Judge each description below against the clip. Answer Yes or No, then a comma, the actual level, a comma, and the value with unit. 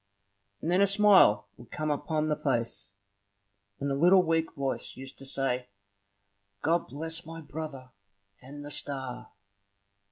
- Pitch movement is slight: No, average, 3.5 semitones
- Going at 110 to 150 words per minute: Yes, average, 140 wpm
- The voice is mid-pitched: Yes, medium, 145 Hz